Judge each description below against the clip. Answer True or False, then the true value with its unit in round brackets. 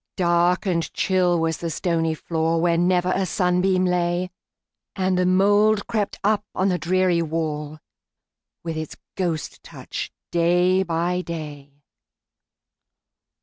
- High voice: False (175 Hz)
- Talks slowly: True (110 wpm)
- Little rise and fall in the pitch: True (2.1 semitones)